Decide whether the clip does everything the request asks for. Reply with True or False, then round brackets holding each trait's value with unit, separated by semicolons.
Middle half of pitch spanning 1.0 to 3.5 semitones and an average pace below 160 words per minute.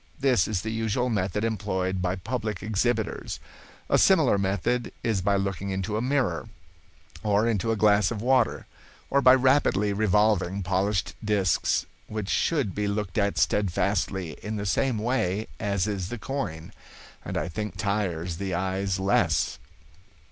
True (2.7 semitones; 150 wpm)